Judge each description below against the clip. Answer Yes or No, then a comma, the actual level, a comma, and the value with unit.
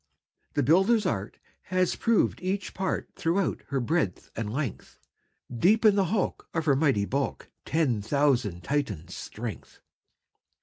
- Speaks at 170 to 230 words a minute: No, slow, 135 wpm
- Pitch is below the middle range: No, medium, 145 Hz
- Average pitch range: No, wide, 8.0 semitones